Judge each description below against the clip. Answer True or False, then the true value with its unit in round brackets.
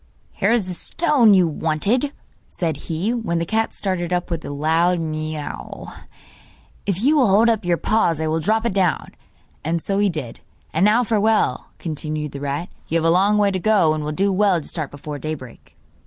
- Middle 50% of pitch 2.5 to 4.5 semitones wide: False (5.0 semitones)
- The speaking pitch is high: False (175 Hz)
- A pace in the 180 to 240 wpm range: True (200 wpm)